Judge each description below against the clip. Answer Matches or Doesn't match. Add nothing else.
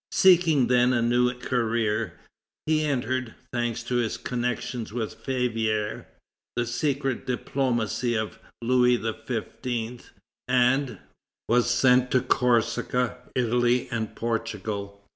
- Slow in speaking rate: Matches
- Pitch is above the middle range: Doesn't match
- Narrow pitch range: Matches